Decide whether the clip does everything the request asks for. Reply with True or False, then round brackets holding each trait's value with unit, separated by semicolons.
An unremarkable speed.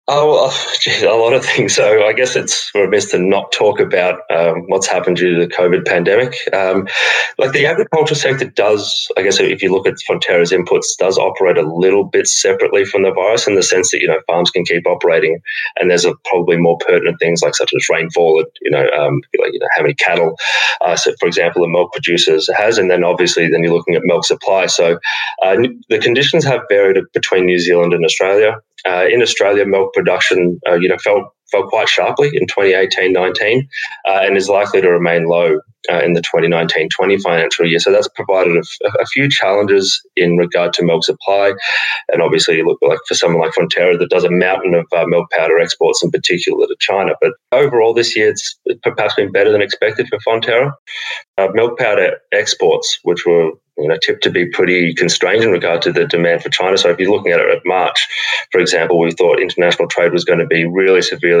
False (215 wpm)